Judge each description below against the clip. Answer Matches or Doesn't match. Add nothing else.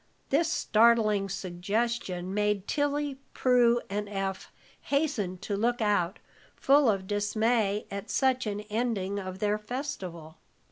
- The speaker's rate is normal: Doesn't match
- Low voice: Doesn't match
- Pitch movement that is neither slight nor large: Matches